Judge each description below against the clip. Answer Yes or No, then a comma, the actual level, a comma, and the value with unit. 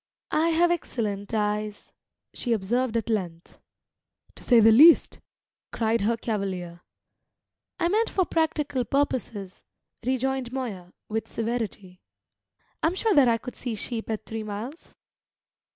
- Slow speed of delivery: Yes, slow, 130 wpm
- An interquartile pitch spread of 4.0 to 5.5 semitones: Yes, average, 4.3 semitones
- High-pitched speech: Yes, high, 230 Hz